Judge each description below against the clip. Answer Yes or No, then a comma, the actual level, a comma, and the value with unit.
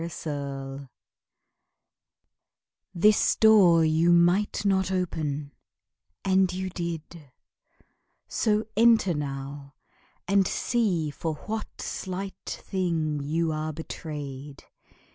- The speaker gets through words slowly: Yes, slow, 90 wpm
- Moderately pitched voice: Yes, medium, 170 Hz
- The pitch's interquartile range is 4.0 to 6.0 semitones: Yes, average, 4.4 semitones